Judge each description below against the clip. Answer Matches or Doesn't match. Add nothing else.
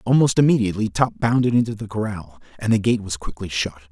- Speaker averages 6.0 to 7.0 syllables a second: Matches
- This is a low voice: Matches